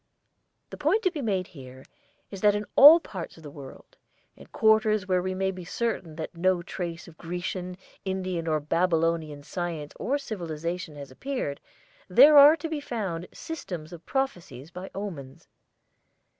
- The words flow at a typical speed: Yes, average, 160 wpm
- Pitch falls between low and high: Yes, medium, 180 Hz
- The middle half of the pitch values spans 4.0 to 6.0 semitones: Yes, average, 4.7 semitones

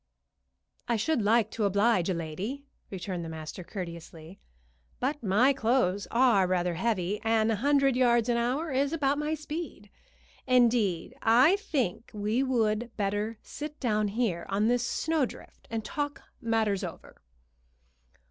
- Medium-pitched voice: No, high, 225 Hz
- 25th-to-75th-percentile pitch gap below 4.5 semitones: No, average, 4.8 semitones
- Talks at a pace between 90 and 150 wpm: Yes, average, 140 wpm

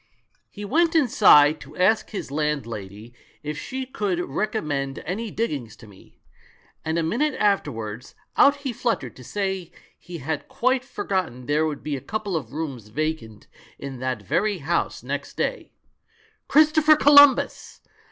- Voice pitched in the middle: Yes, medium, 160 Hz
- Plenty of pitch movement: Yes, wide, 8.4 semitones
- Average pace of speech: Yes, average, 160 wpm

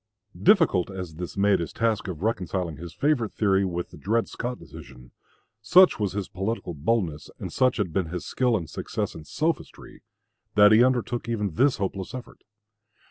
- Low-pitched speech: Yes, low, 100 Hz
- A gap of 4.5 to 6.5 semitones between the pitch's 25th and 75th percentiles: Yes, average, 4.8 semitones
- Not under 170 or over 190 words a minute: Yes, average, 175 wpm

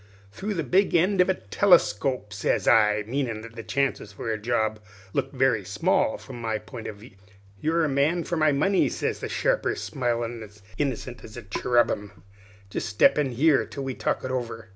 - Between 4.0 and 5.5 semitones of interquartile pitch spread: Yes, average, 5.2 semitones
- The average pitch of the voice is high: No, low, 120 Hz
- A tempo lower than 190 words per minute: No, average, 195 wpm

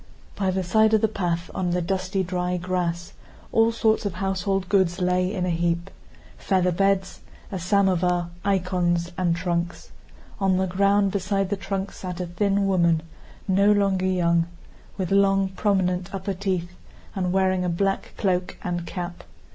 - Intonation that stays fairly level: Yes, narrow, 1.8 semitones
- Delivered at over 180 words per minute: No, average, 155 wpm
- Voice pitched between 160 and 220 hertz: Yes, medium, 185 Hz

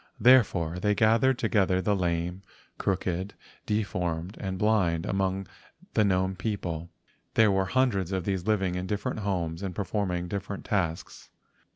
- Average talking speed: Yes, average, 145 wpm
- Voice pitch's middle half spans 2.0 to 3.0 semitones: Yes, narrow, 2.6 semitones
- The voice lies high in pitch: No, very low, 95 Hz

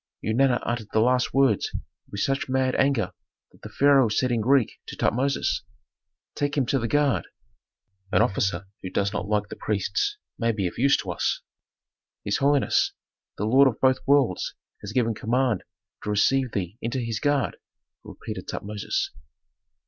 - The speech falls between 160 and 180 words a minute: Yes, average, 165 wpm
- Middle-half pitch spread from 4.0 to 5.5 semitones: Yes, average, 4.4 semitones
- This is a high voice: No, low, 120 Hz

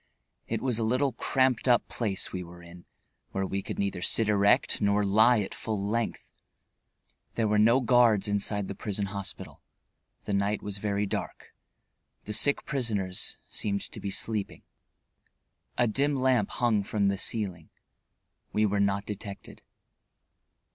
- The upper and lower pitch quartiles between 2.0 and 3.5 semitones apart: Yes, average, 2.7 semitones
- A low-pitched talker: Yes, low, 105 Hz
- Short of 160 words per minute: Yes, average, 150 wpm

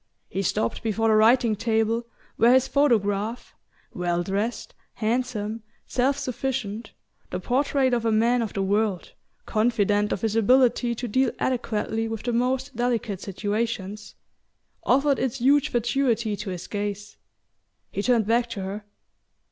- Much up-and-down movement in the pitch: No, average, 3.1 semitones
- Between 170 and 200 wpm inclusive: No, average, 140 wpm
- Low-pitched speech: No, high, 225 Hz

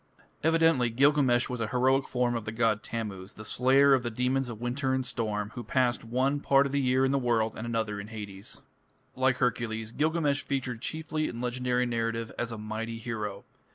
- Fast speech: Yes, fast, 210 wpm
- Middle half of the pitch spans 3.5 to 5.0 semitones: No, average, 2.8 semitones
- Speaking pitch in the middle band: No, low, 120 Hz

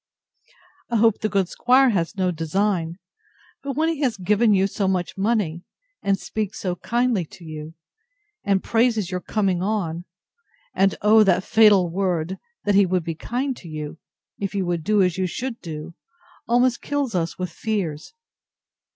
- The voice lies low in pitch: No, high, 195 Hz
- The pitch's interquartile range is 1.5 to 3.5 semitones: No, average, 4.1 semitones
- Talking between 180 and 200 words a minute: No, average, 170 wpm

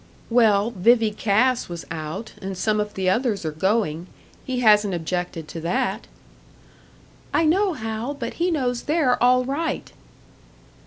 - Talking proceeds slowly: No, average, 145 wpm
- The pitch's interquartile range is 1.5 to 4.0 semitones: No, average, 5.0 semitones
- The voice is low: No, high, 220 Hz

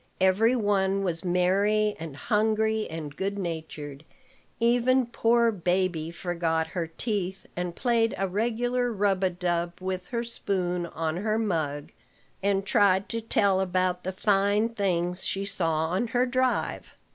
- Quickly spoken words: No, average, 145 wpm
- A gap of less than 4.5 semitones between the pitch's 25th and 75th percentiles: Yes, average, 3.9 semitones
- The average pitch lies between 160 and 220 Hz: Yes, high, 190 Hz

